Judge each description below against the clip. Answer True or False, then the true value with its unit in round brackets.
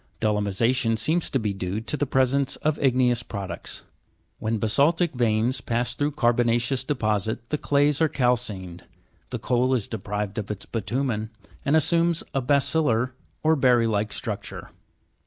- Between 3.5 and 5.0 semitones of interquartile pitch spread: True (4.4 semitones)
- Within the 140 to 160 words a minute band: True (150 wpm)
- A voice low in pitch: True (120 Hz)